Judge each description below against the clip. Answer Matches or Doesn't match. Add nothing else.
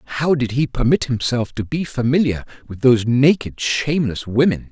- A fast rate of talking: Doesn't match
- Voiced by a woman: Doesn't match